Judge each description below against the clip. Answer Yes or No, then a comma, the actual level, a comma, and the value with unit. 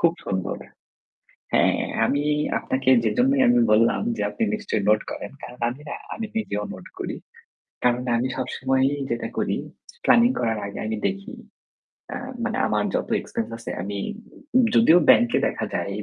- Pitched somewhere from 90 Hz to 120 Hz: No, low, 130 Hz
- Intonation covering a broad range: Yes, wide, 7.8 semitones